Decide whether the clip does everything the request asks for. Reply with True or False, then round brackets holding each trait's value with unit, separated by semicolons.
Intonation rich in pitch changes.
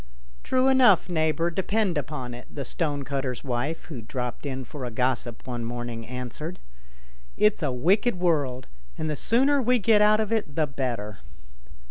True (7.3 semitones)